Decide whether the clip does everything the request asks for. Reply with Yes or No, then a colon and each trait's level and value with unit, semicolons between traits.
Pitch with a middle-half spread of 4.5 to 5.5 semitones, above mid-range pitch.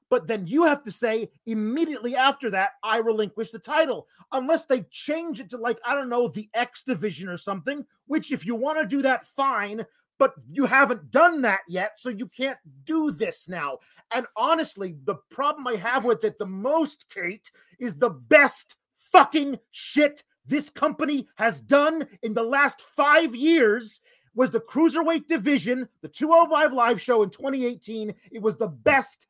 Yes: average, 4.8 semitones; very high, 255 Hz